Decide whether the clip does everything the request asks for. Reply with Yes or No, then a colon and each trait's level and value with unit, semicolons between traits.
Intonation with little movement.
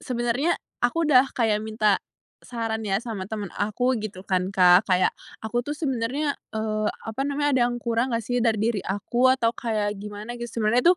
No: average, 3.0 semitones